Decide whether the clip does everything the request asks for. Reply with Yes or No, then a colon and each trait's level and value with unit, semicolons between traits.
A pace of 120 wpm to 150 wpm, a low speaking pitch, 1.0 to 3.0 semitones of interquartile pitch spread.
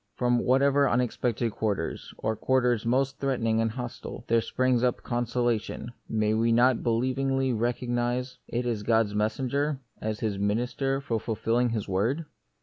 Yes: average, 145 wpm; low, 120 Hz; narrow, 2.4 semitones